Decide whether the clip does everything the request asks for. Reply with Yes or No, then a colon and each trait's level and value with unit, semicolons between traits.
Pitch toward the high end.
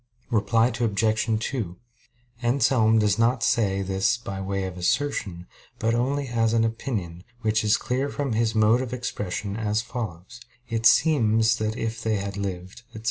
No: low, 110 Hz